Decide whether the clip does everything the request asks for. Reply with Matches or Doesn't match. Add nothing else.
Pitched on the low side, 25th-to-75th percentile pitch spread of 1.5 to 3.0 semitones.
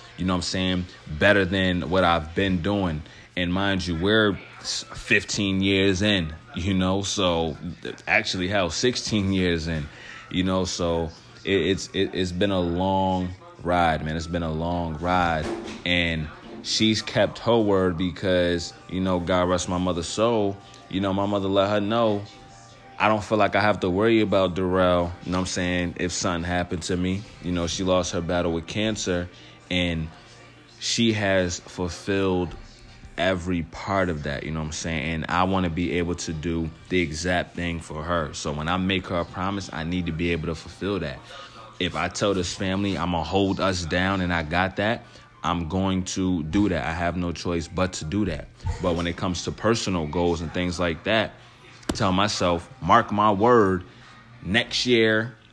Matches